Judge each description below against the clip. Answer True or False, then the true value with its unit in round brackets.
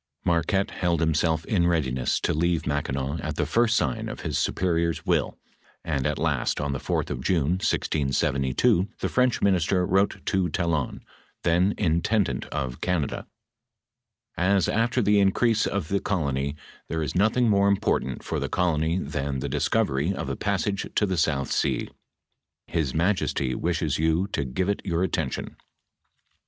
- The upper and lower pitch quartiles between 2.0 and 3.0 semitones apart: False (4.9 semitones)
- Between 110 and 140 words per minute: False (165 wpm)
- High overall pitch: False (85 Hz)